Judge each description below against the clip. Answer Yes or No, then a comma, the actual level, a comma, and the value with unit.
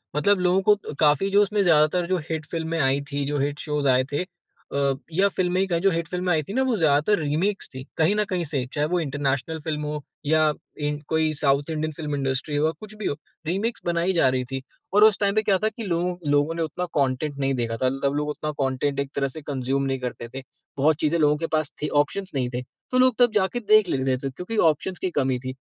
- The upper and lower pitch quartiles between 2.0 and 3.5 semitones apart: No, average, 4.5 semitones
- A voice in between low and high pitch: Yes, medium, 155 Hz